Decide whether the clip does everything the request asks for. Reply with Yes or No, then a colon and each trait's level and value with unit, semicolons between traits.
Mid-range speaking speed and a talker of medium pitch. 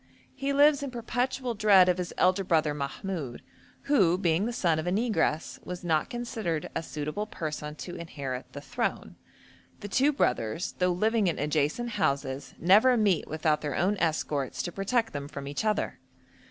Yes: average, 170 wpm; medium, 180 Hz